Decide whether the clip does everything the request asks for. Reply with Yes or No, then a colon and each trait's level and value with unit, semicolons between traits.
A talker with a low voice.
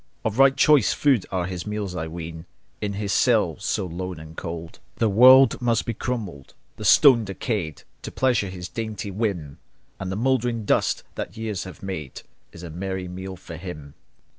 Yes: very low, 95 Hz